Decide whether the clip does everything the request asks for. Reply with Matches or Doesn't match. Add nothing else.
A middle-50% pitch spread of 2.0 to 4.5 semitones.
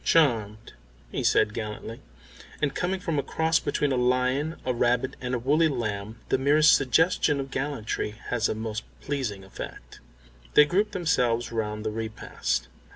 Doesn't match